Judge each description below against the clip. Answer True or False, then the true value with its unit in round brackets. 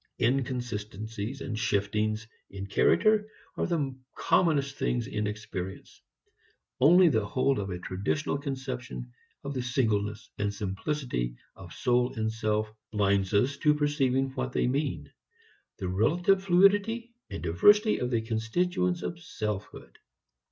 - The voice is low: True (125 Hz)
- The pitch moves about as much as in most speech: False (6.0 semitones)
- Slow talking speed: True (130 wpm)